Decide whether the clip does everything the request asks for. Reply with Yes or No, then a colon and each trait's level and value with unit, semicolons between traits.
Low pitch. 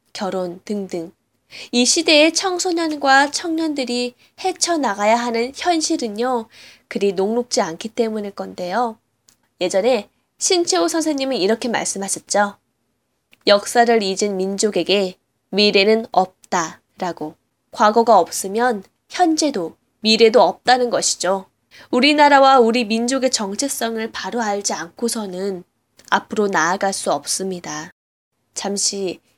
No: high, 220 Hz